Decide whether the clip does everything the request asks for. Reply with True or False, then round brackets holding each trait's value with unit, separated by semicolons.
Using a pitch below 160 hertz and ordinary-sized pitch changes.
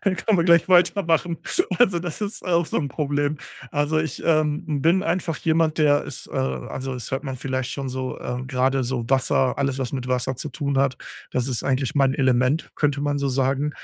True (140 Hz; 3.6 semitones)